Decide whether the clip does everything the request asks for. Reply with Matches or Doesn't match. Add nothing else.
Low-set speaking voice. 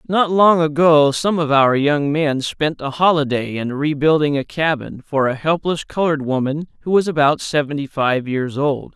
Doesn't match